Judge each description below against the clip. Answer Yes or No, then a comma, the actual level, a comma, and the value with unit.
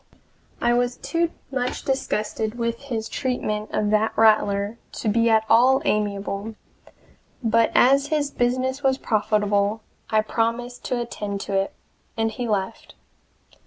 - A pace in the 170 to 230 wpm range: No, slow, 135 wpm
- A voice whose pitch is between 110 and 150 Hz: No, high, 225 Hz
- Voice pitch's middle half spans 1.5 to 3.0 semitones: Yes, average, 2.7 semitones